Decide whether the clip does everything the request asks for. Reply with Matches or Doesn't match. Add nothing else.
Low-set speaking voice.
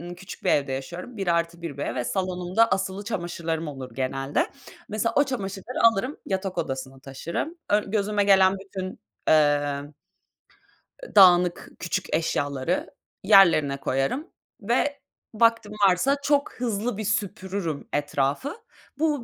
Doesn't match